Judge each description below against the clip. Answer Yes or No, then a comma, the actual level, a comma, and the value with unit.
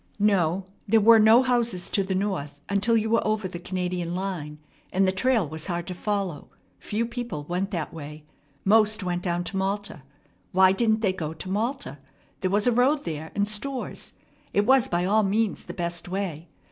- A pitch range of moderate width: Yes, average, 3.7 semitones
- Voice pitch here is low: No, high, 195 Hz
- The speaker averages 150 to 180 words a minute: No, average, 190 wpm